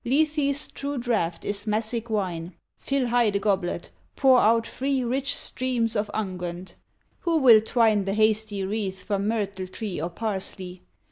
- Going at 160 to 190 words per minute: No, average, 150 wpm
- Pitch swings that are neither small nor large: Yes, average, 4.1 semitones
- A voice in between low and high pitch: No, high, 215 Hz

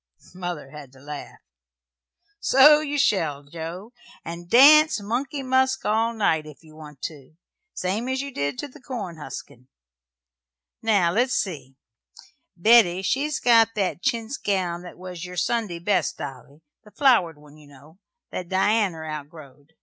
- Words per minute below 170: Yes, average, 150 wpm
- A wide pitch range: Yes, wide, 7.2 semitones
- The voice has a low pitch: No, medium, 180 Hz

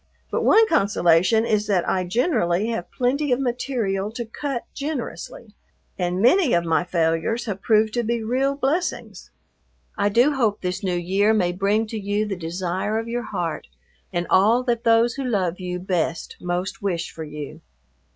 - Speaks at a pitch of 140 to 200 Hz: No, high, 210 Hz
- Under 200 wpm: Yes, average, 170 wpm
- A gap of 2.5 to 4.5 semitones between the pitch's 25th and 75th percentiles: No, average, 4.9 semitones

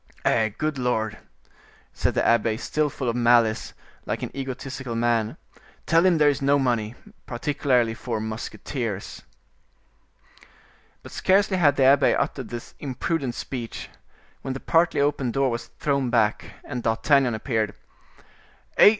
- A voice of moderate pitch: No, low, 125 Hz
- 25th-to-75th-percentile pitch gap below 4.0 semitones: Yes, average, 3.6 semitones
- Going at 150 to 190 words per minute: No, average, 140 wpm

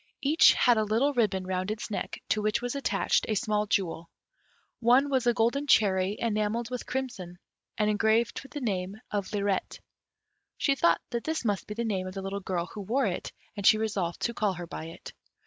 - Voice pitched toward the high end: Yes, high, 215 Hz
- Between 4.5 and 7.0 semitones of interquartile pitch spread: No, average, 3.8 semitones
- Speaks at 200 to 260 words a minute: Yes, fast, 205 wpm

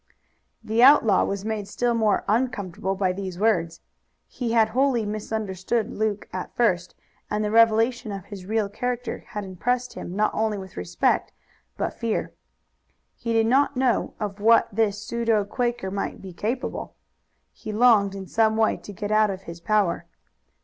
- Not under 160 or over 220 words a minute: Yes, average, 165 wpm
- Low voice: No, high, 215 Hz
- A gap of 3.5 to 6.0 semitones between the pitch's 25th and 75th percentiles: No, average, 2.8 semitones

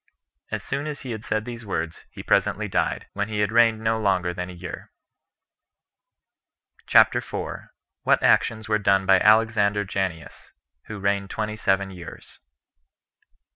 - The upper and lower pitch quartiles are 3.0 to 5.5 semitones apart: No, narrow, 2.4 semitones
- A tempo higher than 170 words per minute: No, average, 150 wpm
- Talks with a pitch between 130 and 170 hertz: No, low, 105 Hz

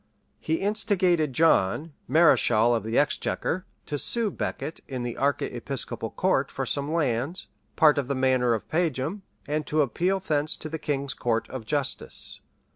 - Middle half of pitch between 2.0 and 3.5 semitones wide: No, average, 4.1 semitones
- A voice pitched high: No, medium, 145 Hz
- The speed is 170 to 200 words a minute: No, average, 155 wpm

